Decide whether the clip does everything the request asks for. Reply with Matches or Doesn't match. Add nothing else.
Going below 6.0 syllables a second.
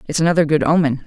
Doesn't match